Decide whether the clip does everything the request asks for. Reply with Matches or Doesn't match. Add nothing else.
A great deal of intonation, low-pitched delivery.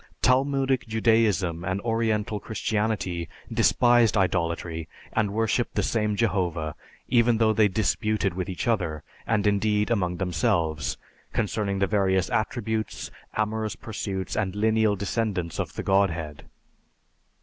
Doesn't match